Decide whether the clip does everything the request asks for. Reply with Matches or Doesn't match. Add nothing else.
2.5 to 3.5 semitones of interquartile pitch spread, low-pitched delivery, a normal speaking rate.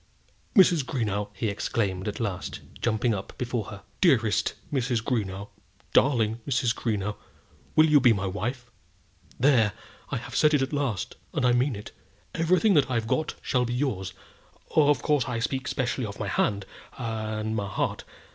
Doesn't match